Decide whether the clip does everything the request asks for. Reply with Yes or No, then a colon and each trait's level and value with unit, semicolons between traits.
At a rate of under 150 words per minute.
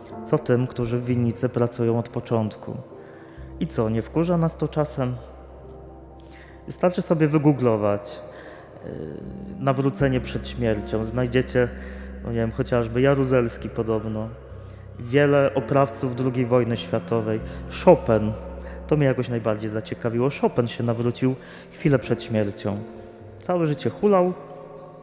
Yes: average, 115 wpm